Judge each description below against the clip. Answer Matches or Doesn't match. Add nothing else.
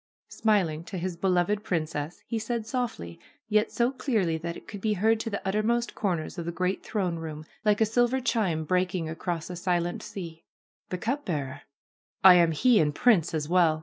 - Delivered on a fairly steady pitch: Doesn't match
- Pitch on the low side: Doesn't match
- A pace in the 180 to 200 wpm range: Matches